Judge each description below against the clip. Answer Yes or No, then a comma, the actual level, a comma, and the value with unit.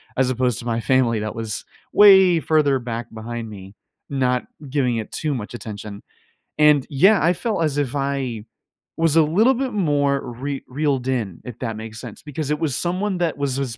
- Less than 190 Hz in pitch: Yes, low, 135 Hz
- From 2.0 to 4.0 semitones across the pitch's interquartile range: No, average, 4.8 semitones